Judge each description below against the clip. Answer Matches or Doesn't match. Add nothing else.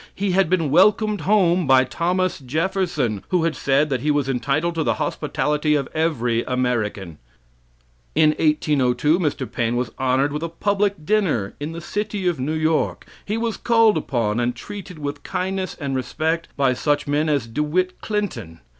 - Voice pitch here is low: Doesn't match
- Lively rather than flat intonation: Matches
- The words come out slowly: Doesn't match